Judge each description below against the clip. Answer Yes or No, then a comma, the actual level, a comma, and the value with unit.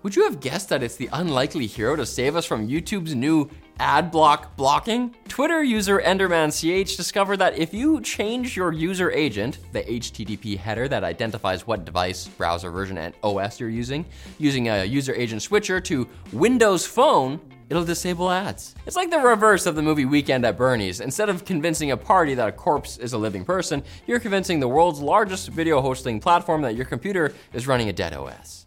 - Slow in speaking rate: No, average, 190 wpm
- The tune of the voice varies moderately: No, wide, 8.6 semitones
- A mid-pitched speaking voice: Yes, medium, 155 Hz